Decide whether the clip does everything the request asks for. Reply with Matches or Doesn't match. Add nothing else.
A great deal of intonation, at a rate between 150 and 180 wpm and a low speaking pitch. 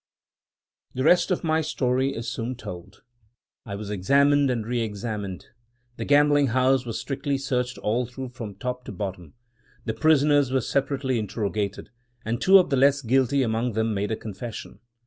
Doesn't match